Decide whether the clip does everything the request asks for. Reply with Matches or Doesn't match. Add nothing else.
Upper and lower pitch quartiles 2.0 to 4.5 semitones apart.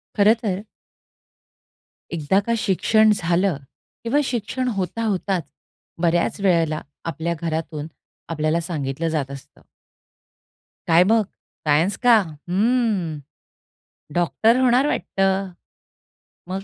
Doesn't match